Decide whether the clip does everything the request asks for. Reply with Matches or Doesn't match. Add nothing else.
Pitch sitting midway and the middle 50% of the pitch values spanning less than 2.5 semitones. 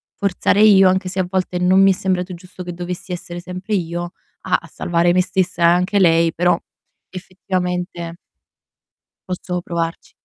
Matches